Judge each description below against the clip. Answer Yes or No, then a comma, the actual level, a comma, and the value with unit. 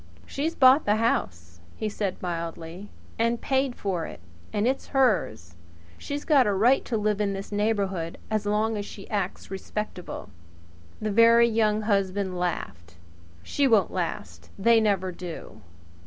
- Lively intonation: No, average, 4.1 semitones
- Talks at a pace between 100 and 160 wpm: Yes, average, 150 wpm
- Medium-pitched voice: No, high, 205 Hz